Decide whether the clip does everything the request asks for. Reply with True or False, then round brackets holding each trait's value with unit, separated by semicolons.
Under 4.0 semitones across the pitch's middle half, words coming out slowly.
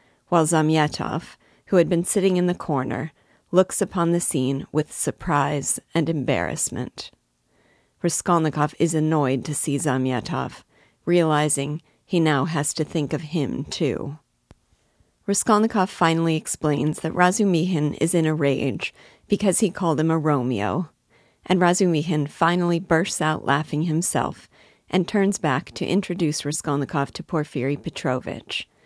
True (3.2 semitones; 130 wpm)